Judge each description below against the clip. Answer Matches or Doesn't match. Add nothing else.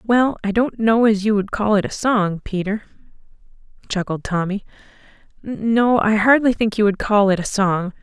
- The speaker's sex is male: Doesn't match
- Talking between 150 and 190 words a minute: Matches